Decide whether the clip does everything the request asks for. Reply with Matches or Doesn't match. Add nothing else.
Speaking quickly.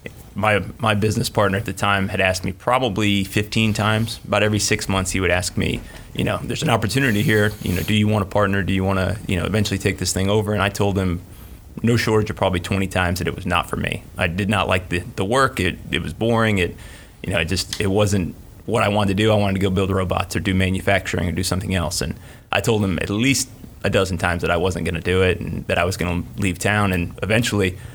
Matches